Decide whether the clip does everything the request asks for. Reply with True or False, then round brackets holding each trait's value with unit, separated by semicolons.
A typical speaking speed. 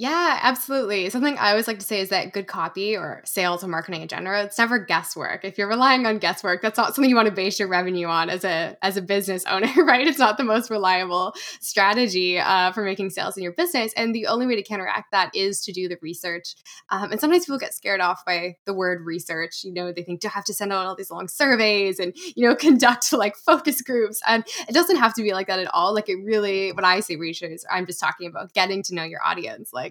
False (255 wpm)